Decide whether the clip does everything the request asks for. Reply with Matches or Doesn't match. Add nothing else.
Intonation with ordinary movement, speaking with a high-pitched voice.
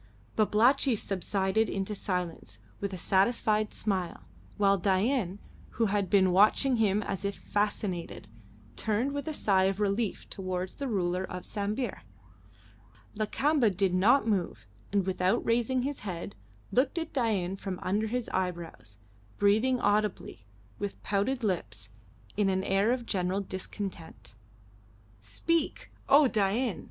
Matches